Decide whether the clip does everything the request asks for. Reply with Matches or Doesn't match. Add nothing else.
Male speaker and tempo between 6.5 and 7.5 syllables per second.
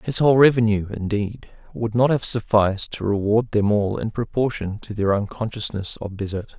Doesn't match